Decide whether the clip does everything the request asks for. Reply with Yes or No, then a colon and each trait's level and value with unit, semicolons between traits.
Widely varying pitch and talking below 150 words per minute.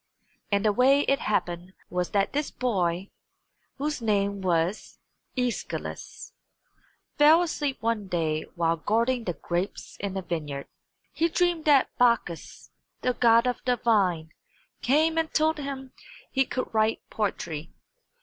Yes: wide, 7.1 semitones; average, 140 wpm